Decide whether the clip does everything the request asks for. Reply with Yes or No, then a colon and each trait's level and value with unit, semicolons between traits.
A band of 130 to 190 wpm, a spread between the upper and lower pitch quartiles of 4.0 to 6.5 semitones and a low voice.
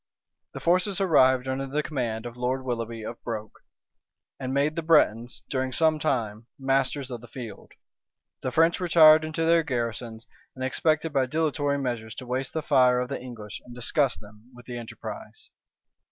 Yes: average, 170 wpm; average, 4.4 semitones; low, 130 Hz